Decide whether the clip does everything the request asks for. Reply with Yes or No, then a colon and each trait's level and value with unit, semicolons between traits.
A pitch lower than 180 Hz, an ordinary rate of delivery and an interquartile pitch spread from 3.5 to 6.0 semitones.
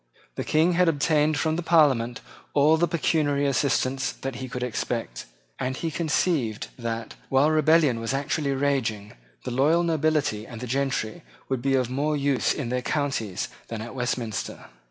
Yes: low, 135 Hz; average, 160 wpm; average, 4.1 semitones